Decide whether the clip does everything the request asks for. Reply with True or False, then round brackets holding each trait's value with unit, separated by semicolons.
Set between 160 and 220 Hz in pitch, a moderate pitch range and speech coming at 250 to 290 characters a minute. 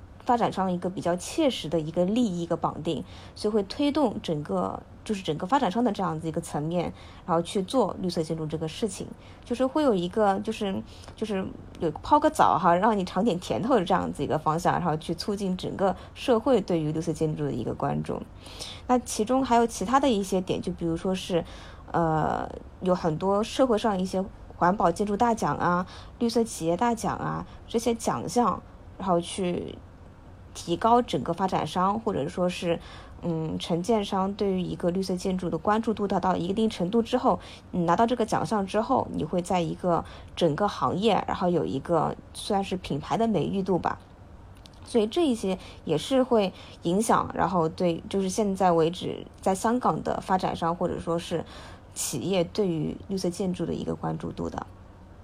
True (185 Hz; 4.7 semitones; 280 characters per minute)